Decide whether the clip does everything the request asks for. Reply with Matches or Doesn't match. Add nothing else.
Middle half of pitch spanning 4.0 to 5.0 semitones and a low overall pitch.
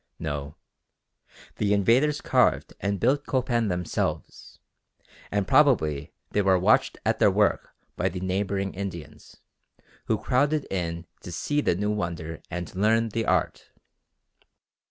Matches